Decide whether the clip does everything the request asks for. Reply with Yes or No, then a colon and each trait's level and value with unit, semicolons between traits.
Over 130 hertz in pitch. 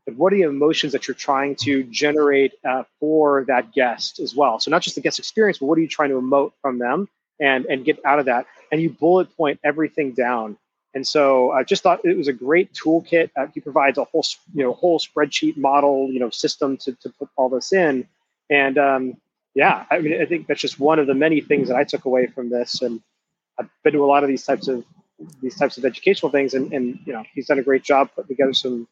Yes: medium, 140 Hz